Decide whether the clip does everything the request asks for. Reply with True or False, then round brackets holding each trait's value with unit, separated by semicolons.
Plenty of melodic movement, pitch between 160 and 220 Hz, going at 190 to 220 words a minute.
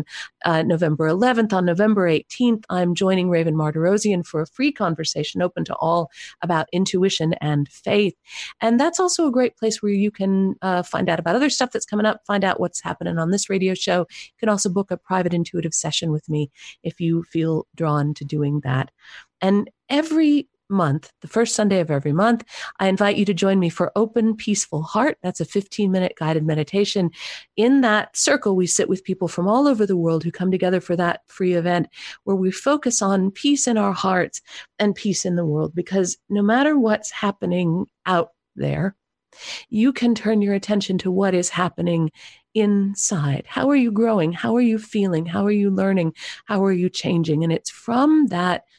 False (3.9 semitones; 190 Hz; 195 wpm)